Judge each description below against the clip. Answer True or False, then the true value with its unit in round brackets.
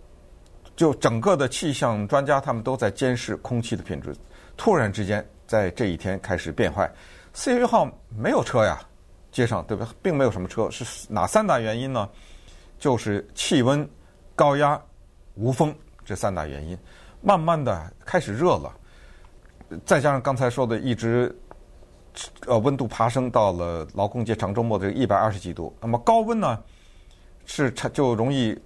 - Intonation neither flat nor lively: False (6.5 semitones)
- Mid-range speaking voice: False (115 Hz)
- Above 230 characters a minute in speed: True (240 characters per minute)